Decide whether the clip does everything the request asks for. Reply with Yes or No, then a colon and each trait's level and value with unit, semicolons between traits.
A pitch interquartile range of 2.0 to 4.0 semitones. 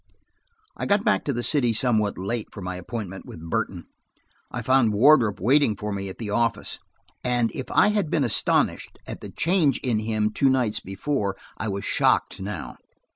No: average, 4.6 semitones